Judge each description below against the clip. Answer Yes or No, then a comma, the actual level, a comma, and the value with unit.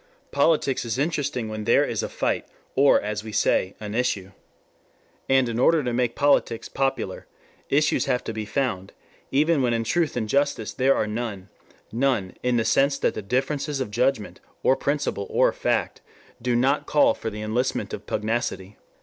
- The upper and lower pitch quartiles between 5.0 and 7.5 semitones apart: No, average, 4.2 semitones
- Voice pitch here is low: Yes, low, 125 Hz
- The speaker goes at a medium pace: Yes, average, 175 wpm